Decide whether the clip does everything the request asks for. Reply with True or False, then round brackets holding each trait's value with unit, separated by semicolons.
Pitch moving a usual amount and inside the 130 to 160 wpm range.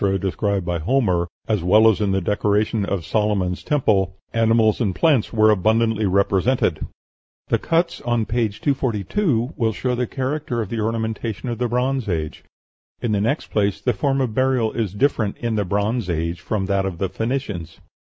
False (3.8 semitones; 175 wpm)